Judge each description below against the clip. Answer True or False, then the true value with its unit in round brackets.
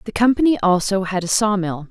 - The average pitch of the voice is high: True (200 Hz)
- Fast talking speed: True (220 wpm)